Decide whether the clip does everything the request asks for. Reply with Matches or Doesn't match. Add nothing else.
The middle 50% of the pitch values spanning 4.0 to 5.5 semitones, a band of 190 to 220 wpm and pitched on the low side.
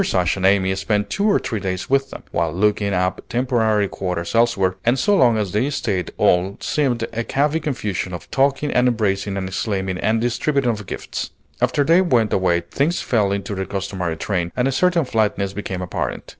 Matches